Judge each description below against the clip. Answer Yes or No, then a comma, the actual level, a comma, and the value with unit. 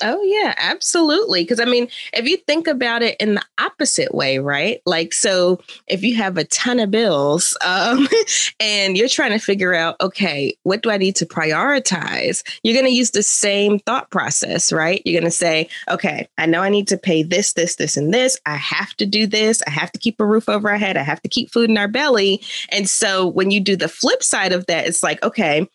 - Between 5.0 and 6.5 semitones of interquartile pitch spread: Yes, wide, 5.4 semitones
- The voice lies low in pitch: No, high, 205 Hz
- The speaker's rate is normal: No, fast, 230 wpm